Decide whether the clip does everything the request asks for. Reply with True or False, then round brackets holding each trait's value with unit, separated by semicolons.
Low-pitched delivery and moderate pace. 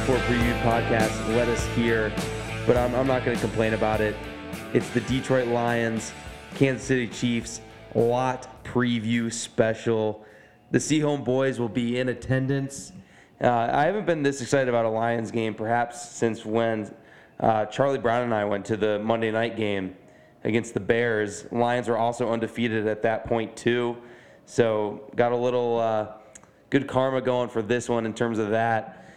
True (115 Hz; 170 wpm)